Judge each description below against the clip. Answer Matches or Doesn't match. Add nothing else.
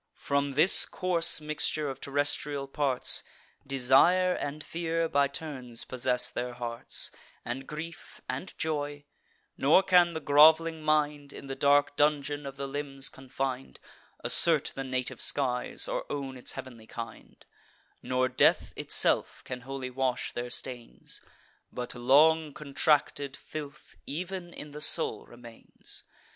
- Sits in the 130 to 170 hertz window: Matches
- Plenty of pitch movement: Doesn't match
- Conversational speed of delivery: Doesn't match